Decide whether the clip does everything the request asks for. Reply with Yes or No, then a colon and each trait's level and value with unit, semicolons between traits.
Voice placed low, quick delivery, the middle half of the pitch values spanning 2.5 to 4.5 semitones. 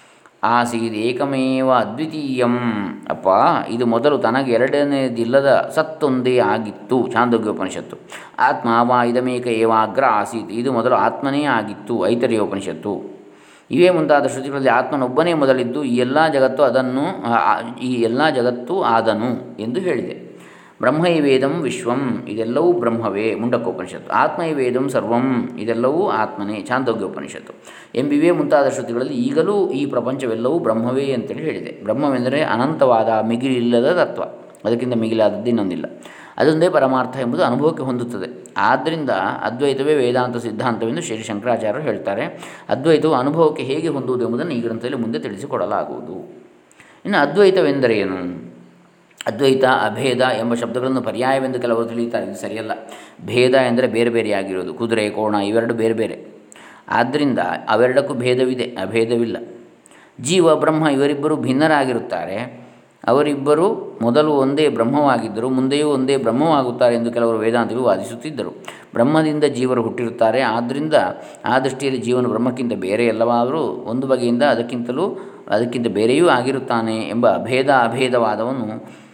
Yes: low, 125 Hz; fast, 110 wpm; average, 2.8 semitones